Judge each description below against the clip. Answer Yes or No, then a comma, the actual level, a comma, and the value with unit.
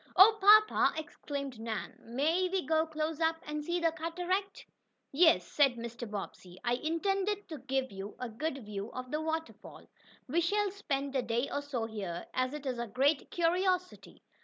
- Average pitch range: No, wide, 5.9 semitones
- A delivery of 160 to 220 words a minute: Yes, average, 175 wpm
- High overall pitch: Yes, very high, 300 Hz